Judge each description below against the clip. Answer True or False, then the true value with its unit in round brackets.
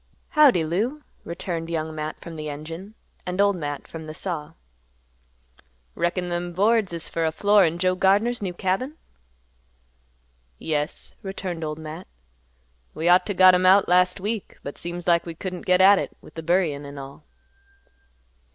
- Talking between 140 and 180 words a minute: True (165 wpm)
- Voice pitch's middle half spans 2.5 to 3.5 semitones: True (3.1 semitones)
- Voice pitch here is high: False (175 Hz)